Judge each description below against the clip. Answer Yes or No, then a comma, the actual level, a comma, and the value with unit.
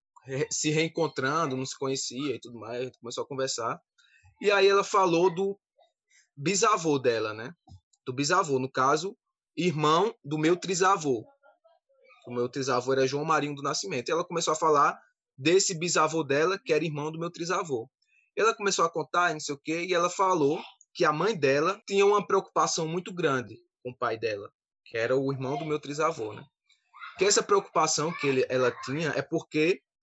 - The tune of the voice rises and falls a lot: Yes, wide, 5.7 semitones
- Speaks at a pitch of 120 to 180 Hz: Yes, medium, 160 Hz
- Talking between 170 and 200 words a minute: Yes, average, 180 wpm